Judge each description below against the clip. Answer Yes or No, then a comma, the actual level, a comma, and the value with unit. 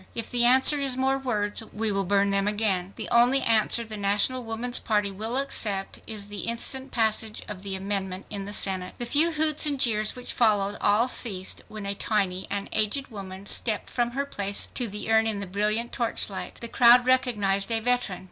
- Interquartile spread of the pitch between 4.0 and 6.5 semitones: No, average, 3.4 semitones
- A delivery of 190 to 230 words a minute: Yes, fast, 205 wpm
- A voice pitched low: No, high, 215 Hz